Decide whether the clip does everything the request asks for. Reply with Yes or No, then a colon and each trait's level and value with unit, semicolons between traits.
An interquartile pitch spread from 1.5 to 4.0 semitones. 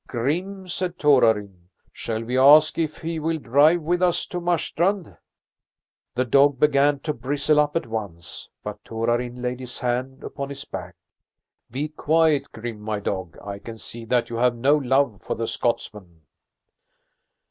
No: average, 5.0 semitones